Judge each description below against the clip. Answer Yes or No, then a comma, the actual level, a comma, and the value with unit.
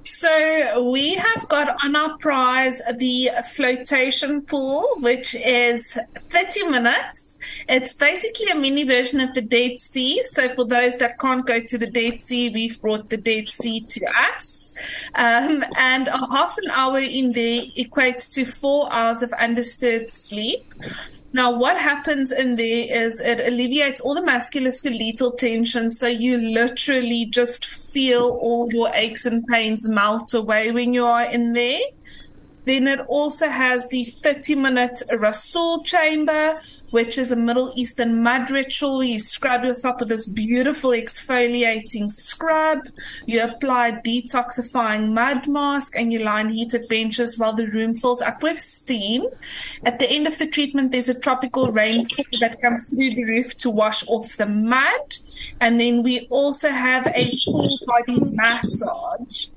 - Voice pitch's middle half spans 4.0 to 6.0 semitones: No, narrow, 2.6 semitones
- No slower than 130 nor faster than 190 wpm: Yes, average, 155 wpm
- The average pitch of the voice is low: No, high, 245 Hz